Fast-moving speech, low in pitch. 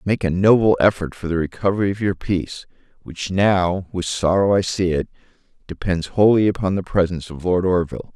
No: average, 185 wpm; very low, 95 Hz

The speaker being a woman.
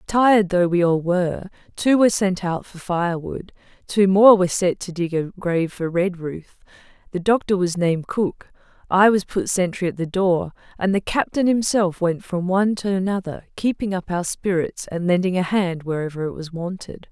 Yes: female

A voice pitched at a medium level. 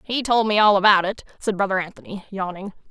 No: high, 200 Hz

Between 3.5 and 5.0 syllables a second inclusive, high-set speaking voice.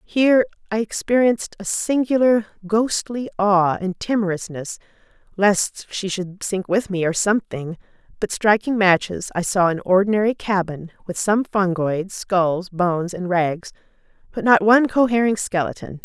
Yes: 4.6 syllables/s; high, 200 Hz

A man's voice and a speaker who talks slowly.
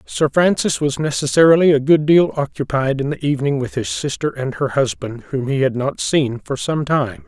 No: male; fast, 205 wpm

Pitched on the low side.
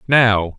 Yes: low, 110 Hz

